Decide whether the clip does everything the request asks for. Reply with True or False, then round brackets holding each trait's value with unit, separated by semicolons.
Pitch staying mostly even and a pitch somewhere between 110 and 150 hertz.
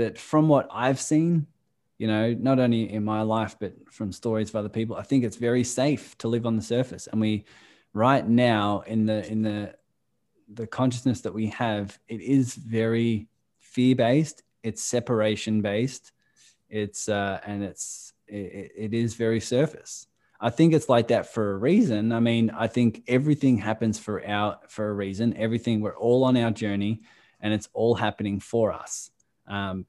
True (2.2 semitones; 115 Hz)